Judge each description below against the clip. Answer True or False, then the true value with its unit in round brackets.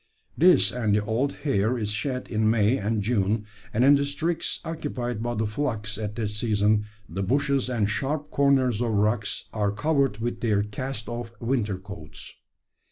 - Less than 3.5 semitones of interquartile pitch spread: False (4.2 semitones)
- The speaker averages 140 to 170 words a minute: True (165 wpm)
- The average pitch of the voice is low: True (115 Hz)